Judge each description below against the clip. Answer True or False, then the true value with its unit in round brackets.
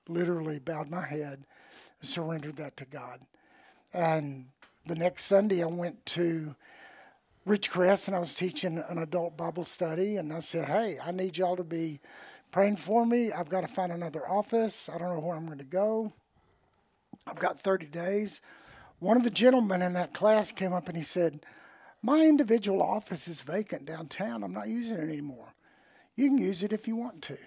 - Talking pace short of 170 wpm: False (190 wpm)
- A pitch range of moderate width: True (3.8 semitones)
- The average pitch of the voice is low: False (180 Hz)